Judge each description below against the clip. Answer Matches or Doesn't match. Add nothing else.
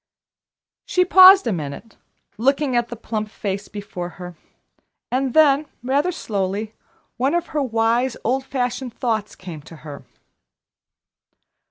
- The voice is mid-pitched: Doesn't match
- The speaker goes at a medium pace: Doesn't match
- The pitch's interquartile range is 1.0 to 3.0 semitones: Doesn't match